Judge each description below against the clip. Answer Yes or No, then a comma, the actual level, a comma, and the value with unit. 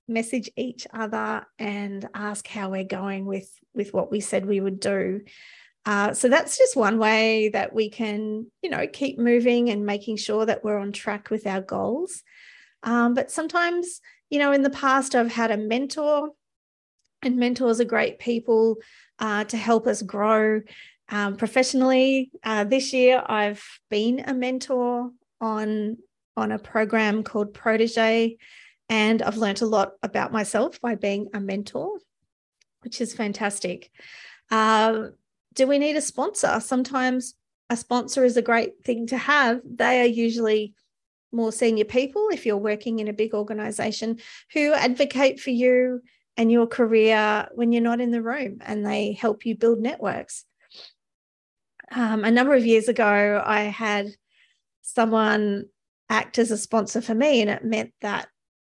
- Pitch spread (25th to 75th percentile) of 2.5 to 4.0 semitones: Yes, average, 2.9 semitones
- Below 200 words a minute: Yes, average, 160 wpm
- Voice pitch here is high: Yes, high, 230 Hz